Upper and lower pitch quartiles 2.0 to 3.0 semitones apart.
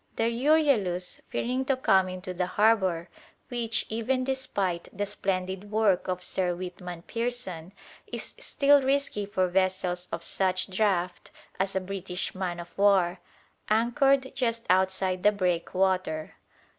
No: average, 4.0 semitones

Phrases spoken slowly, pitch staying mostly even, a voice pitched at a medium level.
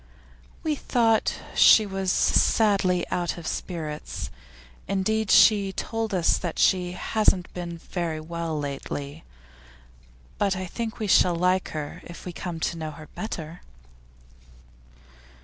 No: slow, 130 wpm; average, 3.5 semitones; medium, 180 Hz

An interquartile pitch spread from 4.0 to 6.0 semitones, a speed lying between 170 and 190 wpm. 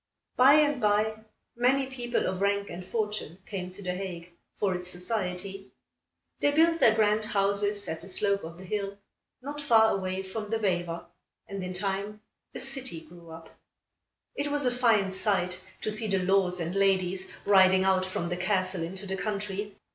No: average, 2.9 semitones; average, 180 wpm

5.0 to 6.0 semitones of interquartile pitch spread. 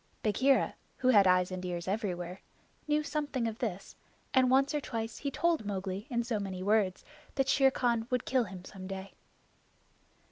Yes: wide, 5.5 semitones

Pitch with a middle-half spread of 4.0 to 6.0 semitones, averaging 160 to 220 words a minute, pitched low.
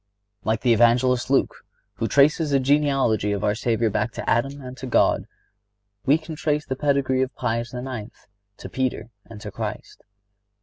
No: average, 3.2 semitones; average, 170 wpm; low, 130 Hz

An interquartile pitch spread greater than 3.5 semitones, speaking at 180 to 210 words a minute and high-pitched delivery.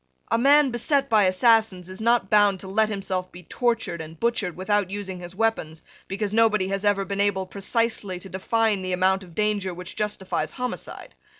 No: average, 3.1 semitones; average, 185 wpm; high, 200 Hz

